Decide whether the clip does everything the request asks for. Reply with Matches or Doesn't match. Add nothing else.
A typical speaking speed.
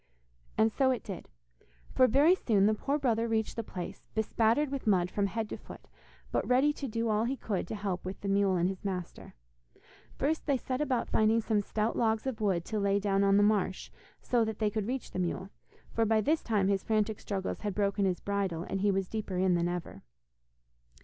Doesn't match